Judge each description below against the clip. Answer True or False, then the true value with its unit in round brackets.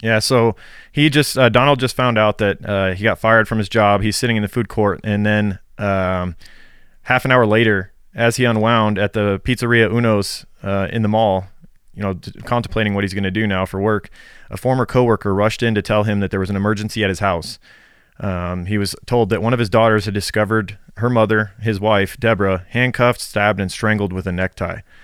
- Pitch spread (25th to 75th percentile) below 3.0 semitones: True (2.6 semitones)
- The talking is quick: True (220 wpm)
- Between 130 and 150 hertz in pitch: False (105 Hz)